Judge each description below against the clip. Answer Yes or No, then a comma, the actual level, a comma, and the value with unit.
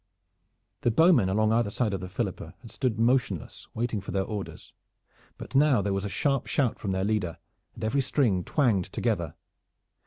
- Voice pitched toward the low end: Yes, low, 110 Hz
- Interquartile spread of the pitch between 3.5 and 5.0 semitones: Yes, average, 4.4 semitones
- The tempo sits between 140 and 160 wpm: No, average, 180 wpm